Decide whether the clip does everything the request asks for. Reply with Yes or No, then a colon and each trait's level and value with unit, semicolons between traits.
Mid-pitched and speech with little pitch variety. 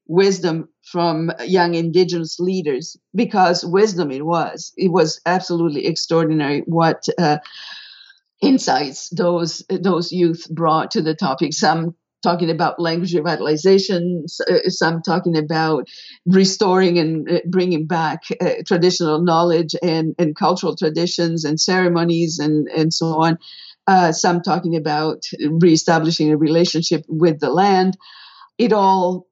Yes: medium, 170 Hz; narrow, 2.2 semitones